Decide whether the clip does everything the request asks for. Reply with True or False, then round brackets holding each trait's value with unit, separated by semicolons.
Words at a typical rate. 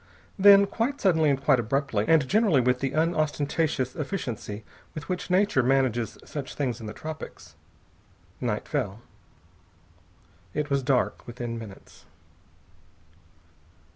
False (120 wpm)